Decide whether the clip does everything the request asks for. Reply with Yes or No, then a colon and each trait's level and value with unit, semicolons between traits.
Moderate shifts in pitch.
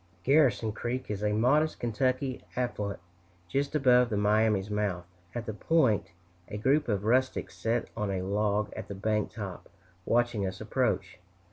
Yes: average, 3.5 semitones